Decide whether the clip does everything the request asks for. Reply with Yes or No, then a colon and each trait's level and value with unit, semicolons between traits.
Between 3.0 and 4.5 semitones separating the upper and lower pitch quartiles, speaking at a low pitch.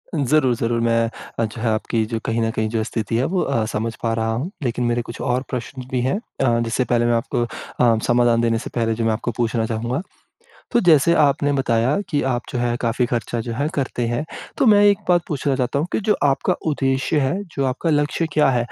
Yes: average, 3.5 semitones; low, 120 Hz